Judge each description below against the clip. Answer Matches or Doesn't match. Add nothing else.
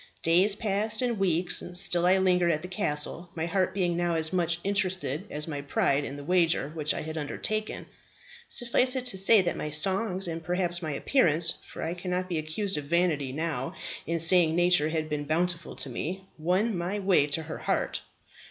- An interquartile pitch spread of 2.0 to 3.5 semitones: Matches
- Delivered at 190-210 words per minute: Matches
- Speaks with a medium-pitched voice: Matches